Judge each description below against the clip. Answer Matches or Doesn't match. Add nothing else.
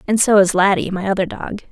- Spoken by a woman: Matches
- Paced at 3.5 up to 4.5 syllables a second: Doesn't match